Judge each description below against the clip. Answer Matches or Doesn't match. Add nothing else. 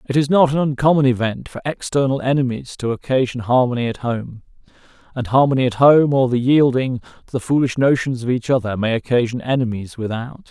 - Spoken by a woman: Doesn't match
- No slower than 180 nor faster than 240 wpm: Matches